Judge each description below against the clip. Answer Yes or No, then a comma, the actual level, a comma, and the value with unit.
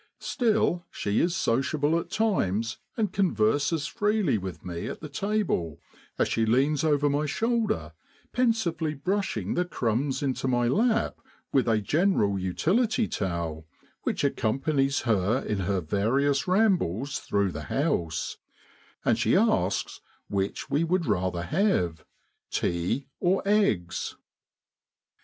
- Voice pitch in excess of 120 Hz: Yes, medium, 140 Hz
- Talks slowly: Yes, slow, 125 wpm